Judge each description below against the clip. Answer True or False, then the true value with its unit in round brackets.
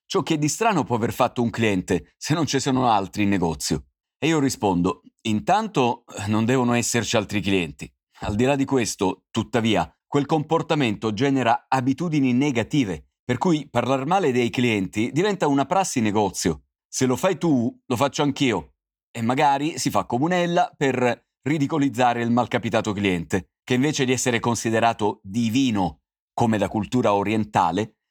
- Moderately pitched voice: False (120 Hz)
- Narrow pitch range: False (5.1 semitones)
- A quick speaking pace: False (155 wpm)